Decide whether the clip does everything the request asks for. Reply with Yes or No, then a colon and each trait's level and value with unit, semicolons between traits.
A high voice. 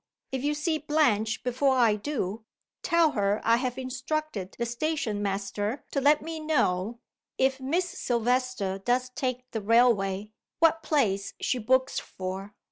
Yes: very high, 250 Hz